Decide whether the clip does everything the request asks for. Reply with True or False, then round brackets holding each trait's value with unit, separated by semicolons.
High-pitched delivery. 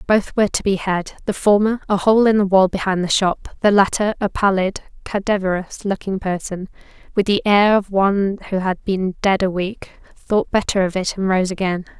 True (195 Hz)